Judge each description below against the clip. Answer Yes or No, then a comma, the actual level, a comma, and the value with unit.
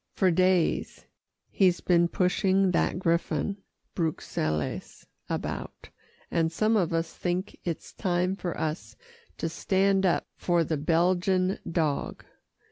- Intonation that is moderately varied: No, narrow, 2.3 semitones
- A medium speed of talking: No, slow, 120 wpm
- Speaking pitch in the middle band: Yes, medium, 175 Hz